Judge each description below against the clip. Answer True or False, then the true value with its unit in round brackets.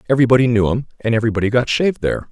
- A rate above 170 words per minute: True (205 wpm)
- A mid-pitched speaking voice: False (120 Hz)